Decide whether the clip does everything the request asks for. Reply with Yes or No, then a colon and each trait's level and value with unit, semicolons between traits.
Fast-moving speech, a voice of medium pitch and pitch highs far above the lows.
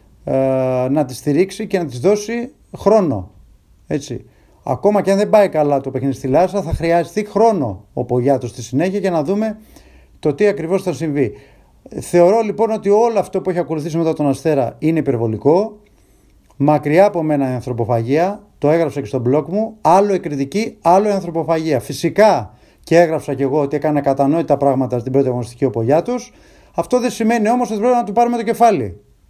Yes: fast, 180 wpm; medium, 160 Hz; wide, 6.8 semitones